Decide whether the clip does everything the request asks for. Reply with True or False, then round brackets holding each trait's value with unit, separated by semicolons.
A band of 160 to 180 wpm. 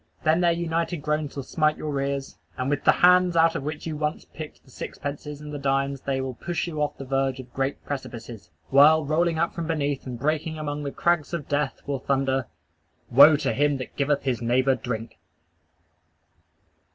False (195 wpm)